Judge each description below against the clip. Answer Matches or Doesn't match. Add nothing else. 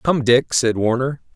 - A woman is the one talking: Doesn't match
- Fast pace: Doesn't match